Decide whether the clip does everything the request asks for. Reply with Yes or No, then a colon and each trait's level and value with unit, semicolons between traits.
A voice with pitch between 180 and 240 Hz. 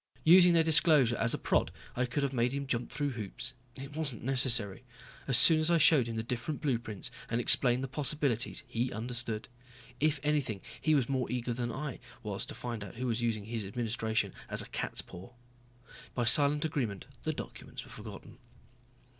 No: low, 125 Hz